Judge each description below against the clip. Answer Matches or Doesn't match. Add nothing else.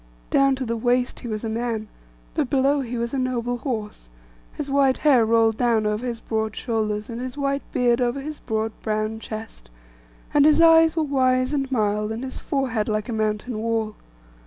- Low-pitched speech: Doesn't match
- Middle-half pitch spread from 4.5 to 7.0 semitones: Doesn't match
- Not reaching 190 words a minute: Doesn't match